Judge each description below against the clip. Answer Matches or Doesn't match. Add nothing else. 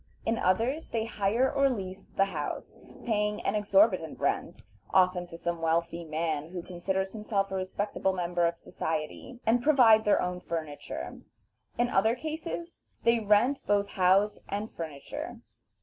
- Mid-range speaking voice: Doesn't match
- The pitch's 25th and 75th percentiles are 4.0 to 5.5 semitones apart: Matches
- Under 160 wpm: Matches